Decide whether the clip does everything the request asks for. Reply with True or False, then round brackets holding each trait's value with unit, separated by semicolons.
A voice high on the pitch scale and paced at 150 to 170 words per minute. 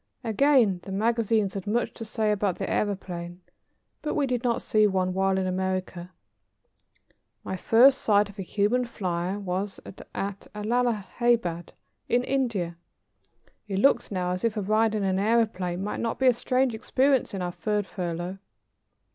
True (205 Hz; 160 wpm)